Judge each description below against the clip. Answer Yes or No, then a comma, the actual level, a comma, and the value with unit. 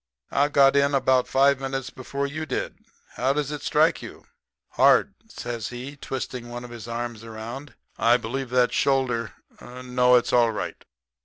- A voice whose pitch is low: Yes, low, 125 Hz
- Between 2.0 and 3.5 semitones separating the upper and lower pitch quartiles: Yes, narrow, 2.4 semitones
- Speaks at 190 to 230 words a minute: No, average, 165 wpm